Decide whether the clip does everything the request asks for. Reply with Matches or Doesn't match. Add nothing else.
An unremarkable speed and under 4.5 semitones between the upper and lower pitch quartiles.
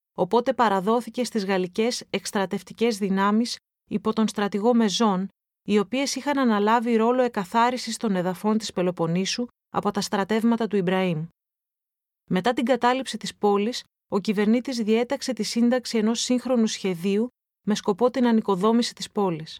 Matches